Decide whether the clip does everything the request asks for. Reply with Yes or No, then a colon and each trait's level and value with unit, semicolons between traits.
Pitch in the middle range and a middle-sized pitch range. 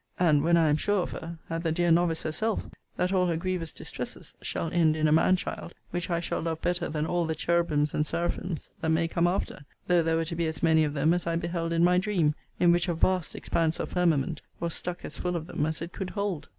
No: medium, 170 Hz; narrow, 1.8 semitones